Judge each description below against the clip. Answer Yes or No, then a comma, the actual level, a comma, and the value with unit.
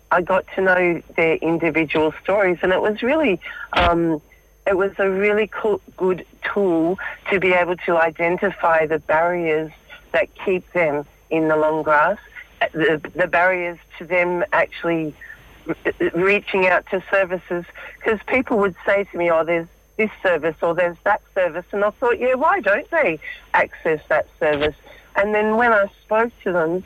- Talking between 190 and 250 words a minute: No, average, 170 wpm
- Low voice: No, medium, 180 Hz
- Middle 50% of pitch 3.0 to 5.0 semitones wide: Yes, average, 3.5 semitones